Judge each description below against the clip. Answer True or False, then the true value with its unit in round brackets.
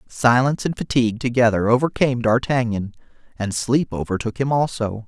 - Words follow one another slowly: True (130 wpm)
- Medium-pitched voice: False (120 Hz)